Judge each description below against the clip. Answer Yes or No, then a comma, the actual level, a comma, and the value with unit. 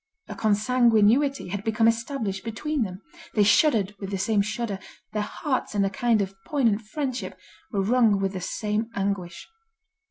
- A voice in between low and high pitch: No, high, 215 Hz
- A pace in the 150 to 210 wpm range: Yes, average, 160 wpm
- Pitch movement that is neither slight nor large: Yes, average, 3.2 semitones